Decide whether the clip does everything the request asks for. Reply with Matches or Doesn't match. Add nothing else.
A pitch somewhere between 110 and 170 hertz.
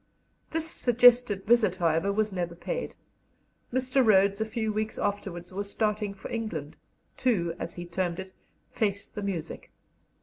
Doesn't match